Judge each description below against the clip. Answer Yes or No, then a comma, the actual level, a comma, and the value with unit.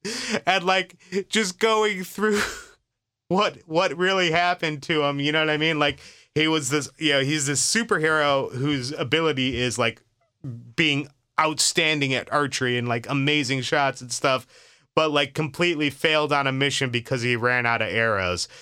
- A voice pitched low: No, medium, 150 Hz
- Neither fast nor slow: Yes, average, 170 wpm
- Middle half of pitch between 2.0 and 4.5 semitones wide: Yes, average, 4.2 semitones